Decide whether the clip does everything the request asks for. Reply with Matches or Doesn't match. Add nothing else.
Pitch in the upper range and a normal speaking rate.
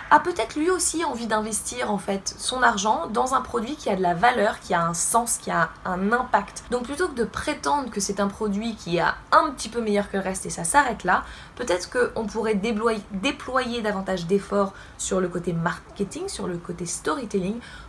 Matches